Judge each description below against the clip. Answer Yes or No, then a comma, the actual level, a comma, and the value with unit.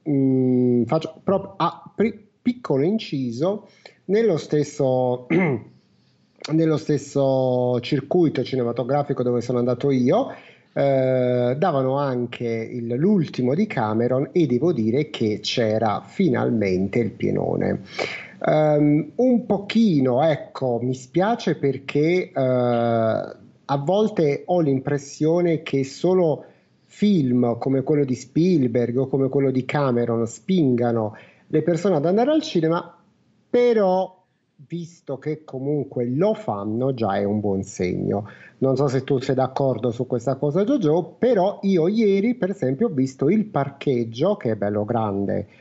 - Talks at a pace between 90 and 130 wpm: Yes, average, 125 wpm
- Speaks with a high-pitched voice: No, medium, 140 Hz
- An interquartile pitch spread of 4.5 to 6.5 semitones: Yes, wide, 5.6 semitones